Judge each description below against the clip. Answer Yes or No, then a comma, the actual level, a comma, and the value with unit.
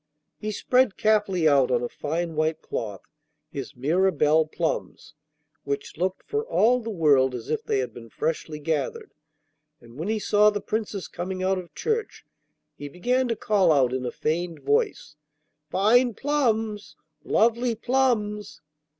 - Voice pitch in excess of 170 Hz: Yes, medium, 185 Hz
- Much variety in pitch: Yes, wide, 6.9 semitones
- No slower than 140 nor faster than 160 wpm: Yes, average, 150 wpm